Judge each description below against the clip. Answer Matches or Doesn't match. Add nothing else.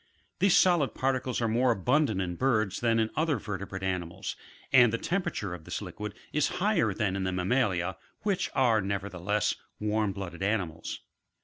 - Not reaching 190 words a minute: Matches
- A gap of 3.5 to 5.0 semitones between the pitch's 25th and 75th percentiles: Doesn't match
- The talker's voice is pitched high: Doesn't match